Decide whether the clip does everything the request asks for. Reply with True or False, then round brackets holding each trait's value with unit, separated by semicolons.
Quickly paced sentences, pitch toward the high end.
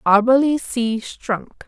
False (105 wpm; 240 Hz)